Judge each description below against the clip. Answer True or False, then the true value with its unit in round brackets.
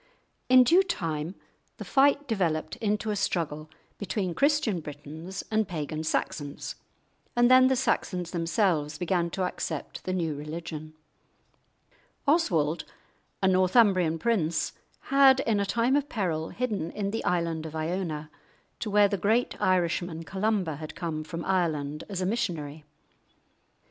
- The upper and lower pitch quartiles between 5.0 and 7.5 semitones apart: True (5.3 semitones)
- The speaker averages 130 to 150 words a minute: True (140 wpm)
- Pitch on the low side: False (180 Hz)